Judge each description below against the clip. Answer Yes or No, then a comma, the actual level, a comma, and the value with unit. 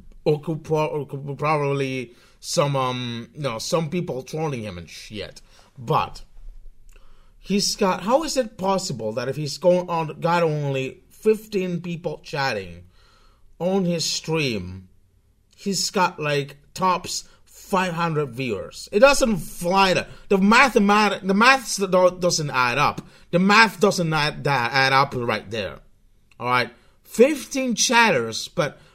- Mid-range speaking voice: Yes, medium, 160 Hz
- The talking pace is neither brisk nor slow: No, slow, 130 wpm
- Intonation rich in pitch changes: Yes, wide, 6.3 semitones